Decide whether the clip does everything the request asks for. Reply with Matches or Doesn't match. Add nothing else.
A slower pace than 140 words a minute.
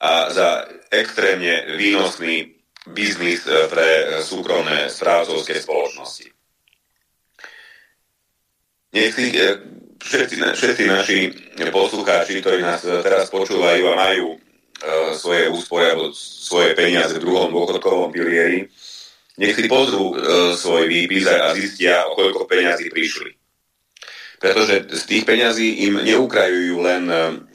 Matches